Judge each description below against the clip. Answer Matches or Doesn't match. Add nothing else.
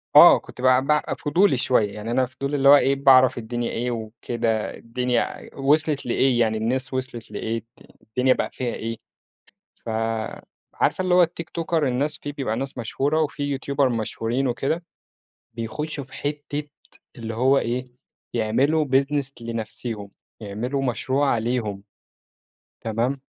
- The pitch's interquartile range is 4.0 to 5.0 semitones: Doesn't match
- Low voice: Matches